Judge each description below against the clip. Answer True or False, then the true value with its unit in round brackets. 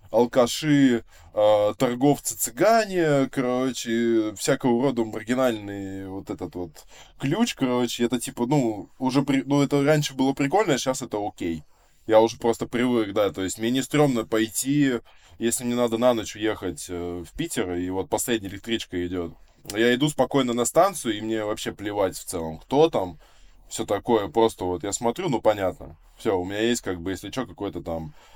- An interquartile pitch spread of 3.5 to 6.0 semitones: True (4.6 semitones)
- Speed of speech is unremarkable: False (170 wpm)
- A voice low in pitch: True (115 Hz)